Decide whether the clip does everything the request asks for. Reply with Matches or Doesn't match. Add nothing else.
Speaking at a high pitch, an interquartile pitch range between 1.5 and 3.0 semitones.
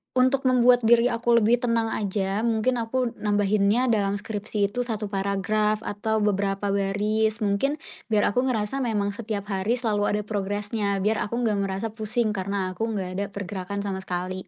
Matches